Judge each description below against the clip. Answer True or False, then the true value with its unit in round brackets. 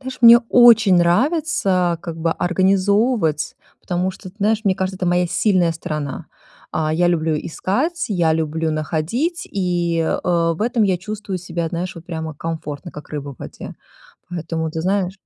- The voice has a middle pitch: True (175 Hz)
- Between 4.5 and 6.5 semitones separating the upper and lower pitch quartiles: False (3.6 semitones)